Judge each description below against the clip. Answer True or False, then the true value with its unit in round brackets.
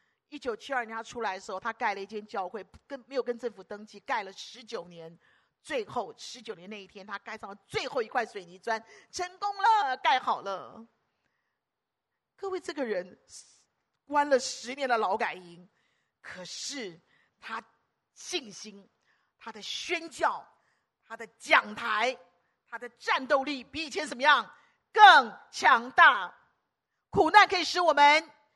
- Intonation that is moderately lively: False (6.5 semitones)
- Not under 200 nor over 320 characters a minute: True (215 characters per minute)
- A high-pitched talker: True (245 Hz)